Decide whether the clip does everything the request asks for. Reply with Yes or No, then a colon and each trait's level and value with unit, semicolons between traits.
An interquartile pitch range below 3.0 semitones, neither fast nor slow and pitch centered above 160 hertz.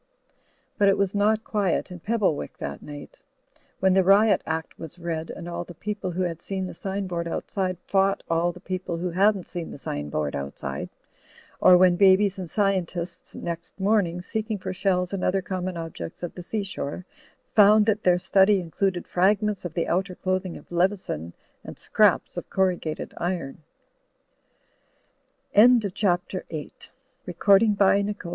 Yes: narrow, 2.5 semitones; average, 150 wpm; medium, 185 Hz